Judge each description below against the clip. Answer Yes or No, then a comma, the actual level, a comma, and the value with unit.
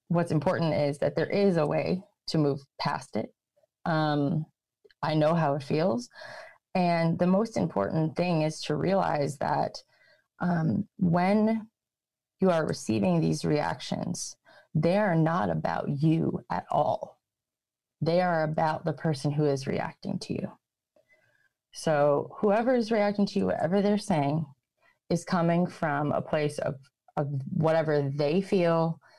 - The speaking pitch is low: No, medium, 165 Hz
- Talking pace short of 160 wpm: Yes, average, 145 wpm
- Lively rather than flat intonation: No, average, 3.9 semitones